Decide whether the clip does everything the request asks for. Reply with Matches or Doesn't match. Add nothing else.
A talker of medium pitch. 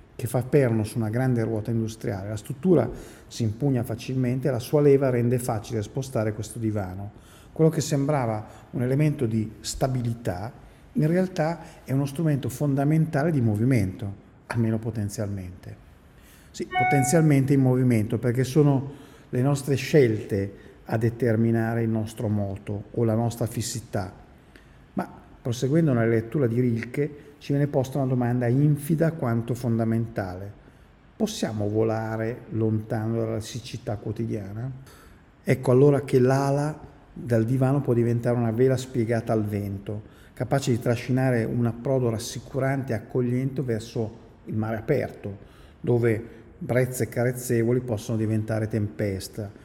Doesn't match